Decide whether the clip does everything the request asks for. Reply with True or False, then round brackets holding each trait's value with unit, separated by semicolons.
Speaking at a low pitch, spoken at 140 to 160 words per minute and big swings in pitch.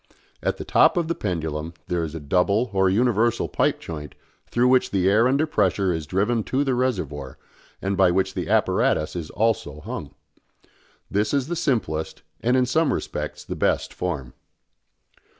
False (100 Hz; 170 wpm; 7.0 semitones)